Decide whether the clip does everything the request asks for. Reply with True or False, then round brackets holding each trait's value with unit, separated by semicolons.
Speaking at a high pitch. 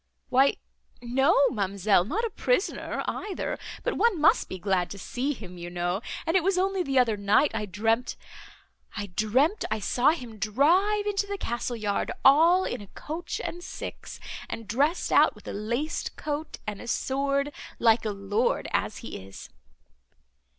True (250 Hz)